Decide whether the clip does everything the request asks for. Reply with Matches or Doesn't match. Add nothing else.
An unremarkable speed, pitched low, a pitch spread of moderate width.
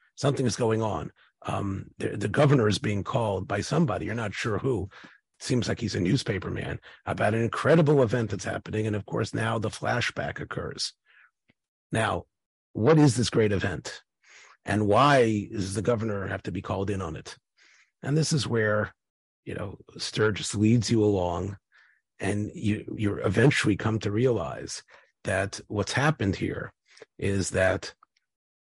Matches